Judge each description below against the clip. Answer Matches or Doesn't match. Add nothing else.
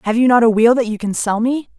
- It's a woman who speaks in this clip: Matches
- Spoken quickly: Matches